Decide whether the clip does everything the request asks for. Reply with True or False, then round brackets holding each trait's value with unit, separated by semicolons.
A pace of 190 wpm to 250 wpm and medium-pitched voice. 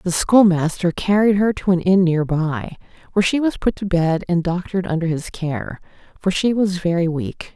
True (200 wpm; 180 Hz)